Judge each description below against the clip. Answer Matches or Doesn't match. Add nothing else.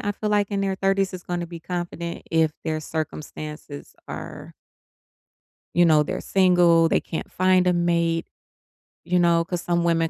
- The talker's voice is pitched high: Doesn't match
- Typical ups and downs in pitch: Doesn't match